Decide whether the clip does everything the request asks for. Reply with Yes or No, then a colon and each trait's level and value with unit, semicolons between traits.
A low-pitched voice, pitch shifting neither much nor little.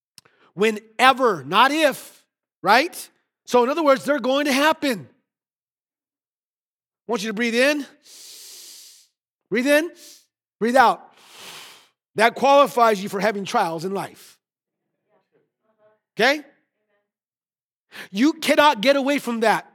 No: very high, 250 Hz; average, 4.8 semitones